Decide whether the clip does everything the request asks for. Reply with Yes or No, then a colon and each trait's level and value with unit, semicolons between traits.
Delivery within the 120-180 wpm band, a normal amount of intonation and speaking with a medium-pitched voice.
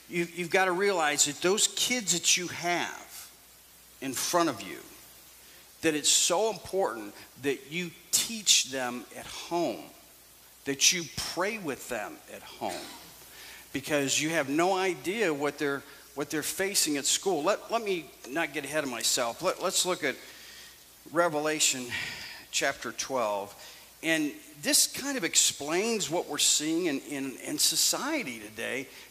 No: average, 145 wpm; wide, 6.4 semitones; medium, 175 Hz